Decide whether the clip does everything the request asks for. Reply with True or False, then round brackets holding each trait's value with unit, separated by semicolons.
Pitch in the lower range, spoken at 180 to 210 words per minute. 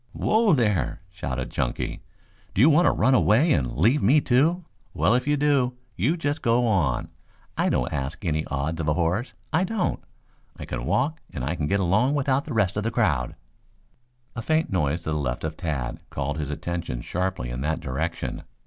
True (95 Hz; 195 wpm)